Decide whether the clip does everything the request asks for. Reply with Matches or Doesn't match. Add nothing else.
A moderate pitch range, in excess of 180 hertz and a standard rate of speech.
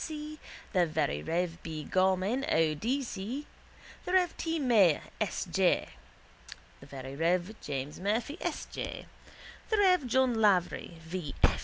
Doesn't match